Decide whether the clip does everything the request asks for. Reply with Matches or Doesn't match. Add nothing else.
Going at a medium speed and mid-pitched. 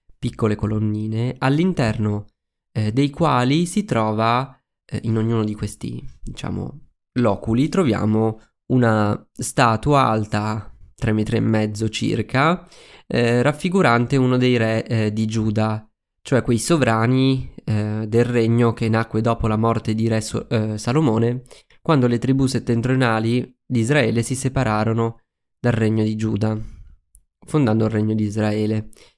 Doesn't match